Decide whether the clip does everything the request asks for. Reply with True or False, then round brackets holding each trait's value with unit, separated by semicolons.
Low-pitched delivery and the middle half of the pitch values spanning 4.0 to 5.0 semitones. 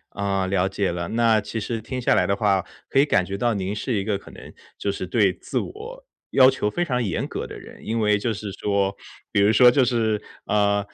False (105 Hz; 3.2 semitones)